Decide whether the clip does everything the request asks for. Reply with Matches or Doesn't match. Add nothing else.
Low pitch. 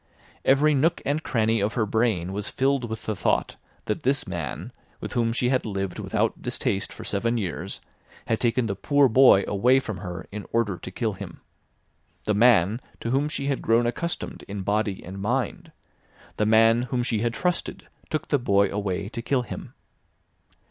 Matches